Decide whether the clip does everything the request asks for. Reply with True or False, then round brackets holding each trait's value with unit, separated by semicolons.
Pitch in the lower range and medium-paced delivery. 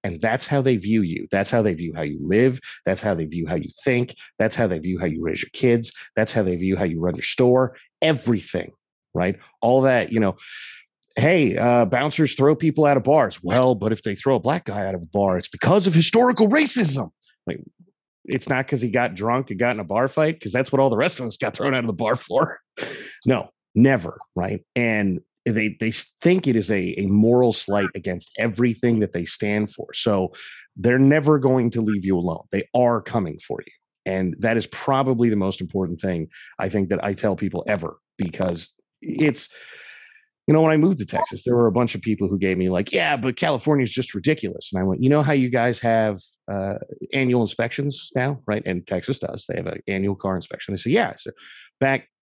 False (115 Hz; 225 wpm)